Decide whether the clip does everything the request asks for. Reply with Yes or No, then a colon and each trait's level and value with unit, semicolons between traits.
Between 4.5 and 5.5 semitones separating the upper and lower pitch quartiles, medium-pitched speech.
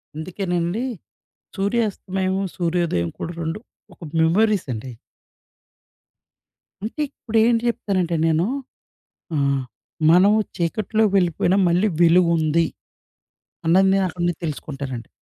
No: average, 3.4 semitones; medium, 175 Hz